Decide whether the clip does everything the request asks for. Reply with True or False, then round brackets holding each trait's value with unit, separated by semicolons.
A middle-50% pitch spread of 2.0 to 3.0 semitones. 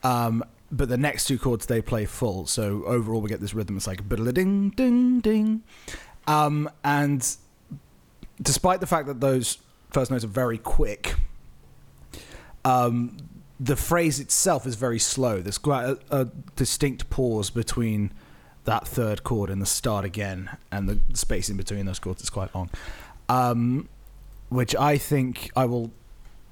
False (4.8 semitones)